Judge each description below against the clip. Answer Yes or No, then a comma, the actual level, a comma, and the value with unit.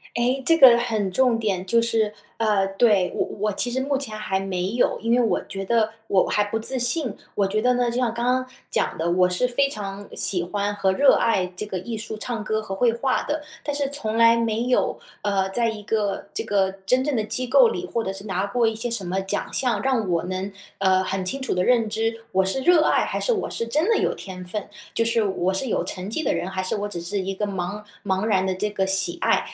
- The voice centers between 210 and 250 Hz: Yes, high, 215 Hz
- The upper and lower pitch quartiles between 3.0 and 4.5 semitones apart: Yes, average, 3.9 semitones